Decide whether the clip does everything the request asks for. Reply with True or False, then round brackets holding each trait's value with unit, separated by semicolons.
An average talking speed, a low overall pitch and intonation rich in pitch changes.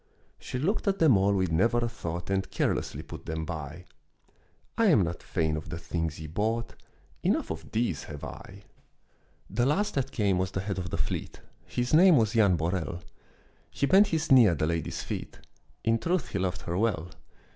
True (195 wpm; 95 Hz; 6.5 semitones)